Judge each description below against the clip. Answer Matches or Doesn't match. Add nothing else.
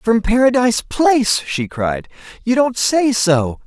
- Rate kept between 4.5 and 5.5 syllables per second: Doesn't match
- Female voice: Doesn't match